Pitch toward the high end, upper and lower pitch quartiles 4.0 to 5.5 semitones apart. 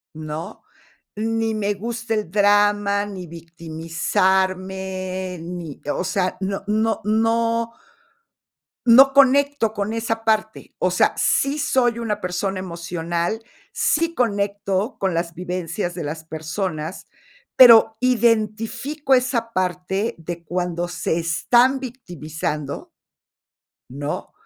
Yes: high, 200 Hz; average, 4.5 semitones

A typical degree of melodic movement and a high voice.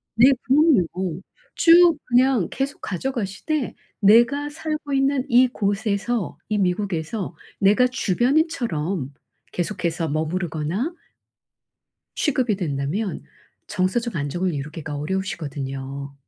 No: wide, 7.7 semitones; high, 200 Hz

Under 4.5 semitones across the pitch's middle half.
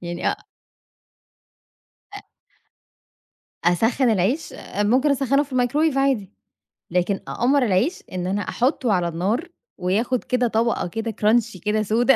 No: average, 5.1 semitones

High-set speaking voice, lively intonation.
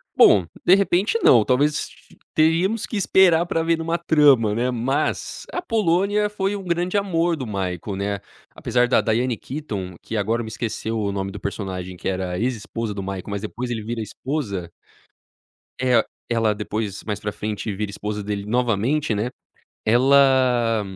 No: low, 120 Hz; wide, 7.2 semitones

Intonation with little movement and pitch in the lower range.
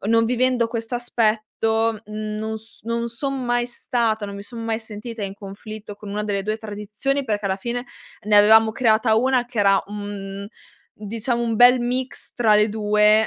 No: narrow, 2.2 semitones; high, 220 Hz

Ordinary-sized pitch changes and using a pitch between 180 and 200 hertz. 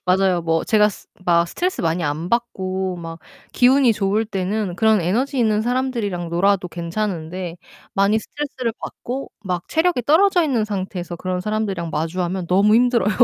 Yes: average, 4.8 semitones; high, 195 Hz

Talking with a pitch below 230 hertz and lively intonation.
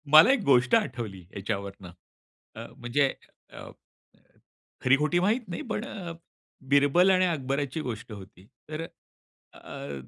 Yes: medium, 140 Hz; wide, 8.3 semitones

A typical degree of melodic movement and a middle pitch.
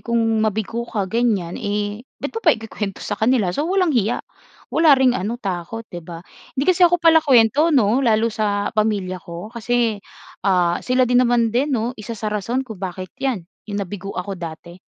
No: average, 4.2 semitones; high, 220 Hz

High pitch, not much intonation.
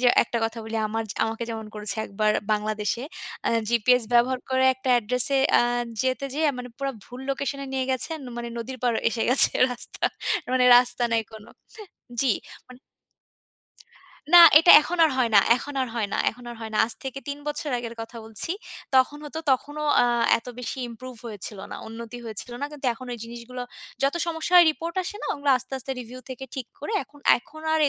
No: very high, 250 Hz; average, 3.1 semitones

